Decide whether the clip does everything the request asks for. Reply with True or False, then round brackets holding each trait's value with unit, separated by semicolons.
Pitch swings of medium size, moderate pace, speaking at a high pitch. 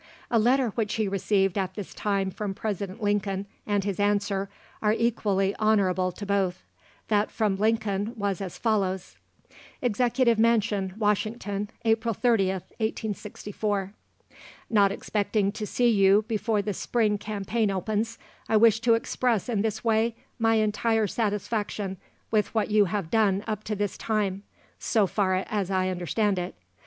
False (2.1 semitones; 145 wpm; 210 Hz)